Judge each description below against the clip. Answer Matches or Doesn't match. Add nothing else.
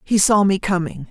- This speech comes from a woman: Matches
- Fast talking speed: Matches